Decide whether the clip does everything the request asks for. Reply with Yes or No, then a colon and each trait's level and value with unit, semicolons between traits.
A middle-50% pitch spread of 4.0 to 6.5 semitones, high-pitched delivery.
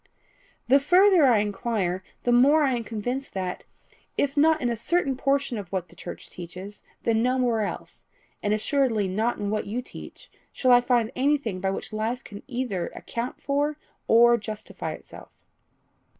Yes: average, 4.6 semitones; high, 240 Hz